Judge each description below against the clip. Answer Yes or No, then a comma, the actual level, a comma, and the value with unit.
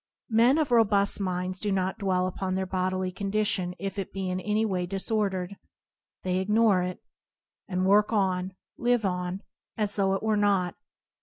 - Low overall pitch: No, high, 195 Hz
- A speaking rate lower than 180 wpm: Yes, average, 165 wpm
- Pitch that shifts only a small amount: Yes, narrow, 2.2 semitones